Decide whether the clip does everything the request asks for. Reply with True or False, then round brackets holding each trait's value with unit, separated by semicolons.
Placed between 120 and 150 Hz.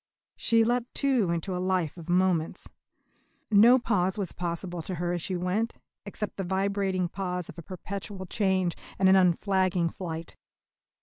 False (185 Hz)